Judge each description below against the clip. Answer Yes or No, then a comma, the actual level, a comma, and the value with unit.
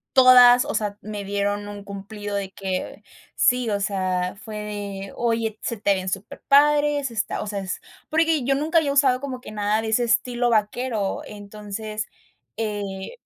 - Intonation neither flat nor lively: Yes, average, 3.6 semitones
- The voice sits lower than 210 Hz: No, high, 215 Hz